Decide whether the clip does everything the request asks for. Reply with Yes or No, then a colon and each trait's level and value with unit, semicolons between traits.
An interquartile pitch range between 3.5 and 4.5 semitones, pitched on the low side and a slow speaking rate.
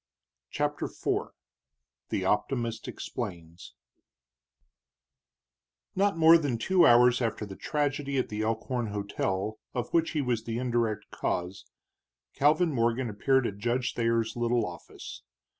Yes: average, 4.1 semitones; low, 120 Hz; slow, 125 wpm